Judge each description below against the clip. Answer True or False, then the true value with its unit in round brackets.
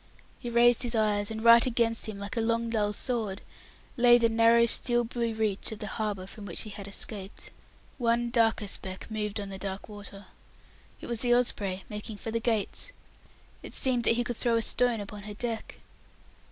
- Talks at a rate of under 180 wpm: False (195 wpm)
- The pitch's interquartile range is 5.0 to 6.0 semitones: False (2.4 semitones)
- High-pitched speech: True (225 Hz)